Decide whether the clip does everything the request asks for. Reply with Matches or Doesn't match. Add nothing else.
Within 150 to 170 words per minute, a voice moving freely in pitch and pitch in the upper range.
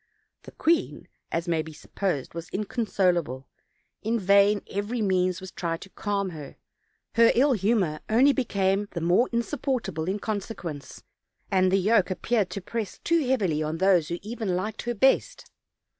Doesn't match